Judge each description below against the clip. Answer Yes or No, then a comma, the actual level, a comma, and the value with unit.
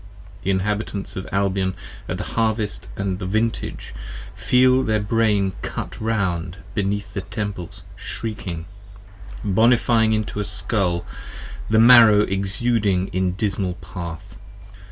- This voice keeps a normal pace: No, slow, 115 wpm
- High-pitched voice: No, low, 100 Hz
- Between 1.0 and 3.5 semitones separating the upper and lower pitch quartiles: Yes, average, 2.8 semitones